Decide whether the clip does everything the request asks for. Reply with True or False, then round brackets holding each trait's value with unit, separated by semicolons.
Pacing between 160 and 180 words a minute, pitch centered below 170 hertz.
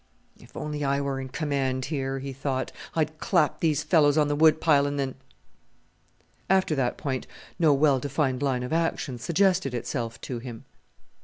True (175 wpm; 140 Hz)